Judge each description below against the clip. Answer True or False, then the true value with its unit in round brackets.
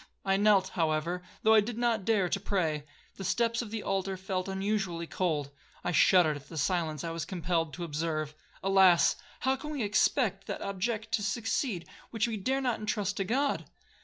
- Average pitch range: True (4.4 semitones)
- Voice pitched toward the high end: True (195 Hz)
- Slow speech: False (185 wpm)